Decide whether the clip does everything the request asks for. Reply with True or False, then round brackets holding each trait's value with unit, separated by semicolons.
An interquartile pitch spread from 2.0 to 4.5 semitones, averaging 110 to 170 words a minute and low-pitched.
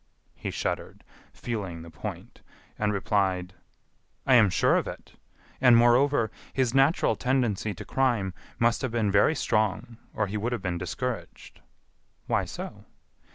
True (4.0 semitones; 145 wpm; 110 Hz)